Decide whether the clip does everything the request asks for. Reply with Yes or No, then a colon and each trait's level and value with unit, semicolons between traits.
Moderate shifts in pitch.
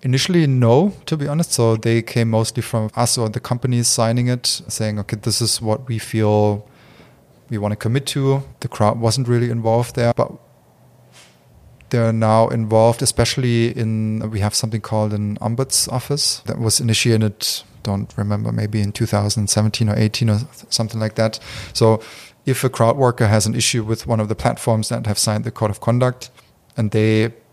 No: narrow, 1.9 semitones